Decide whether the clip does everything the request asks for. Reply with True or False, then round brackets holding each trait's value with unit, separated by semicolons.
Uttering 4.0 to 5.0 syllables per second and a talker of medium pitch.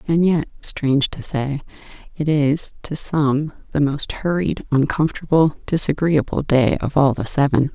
True (4.4 syllables/s; 145 Hz)